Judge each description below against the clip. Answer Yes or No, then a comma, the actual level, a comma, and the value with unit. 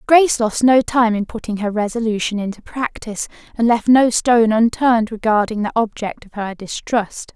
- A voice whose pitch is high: Yes, high, 225 Hz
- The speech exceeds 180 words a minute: No, average, 170 wpm